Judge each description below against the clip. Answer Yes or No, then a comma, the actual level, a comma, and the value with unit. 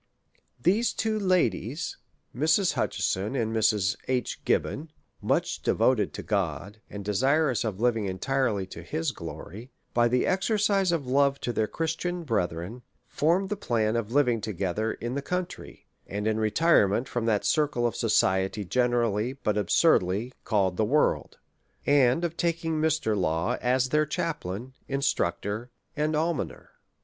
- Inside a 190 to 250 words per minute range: No, average, 145 wpm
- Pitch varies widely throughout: Yes, wide, 6.5 semitones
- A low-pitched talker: Yes, low, 120 Hz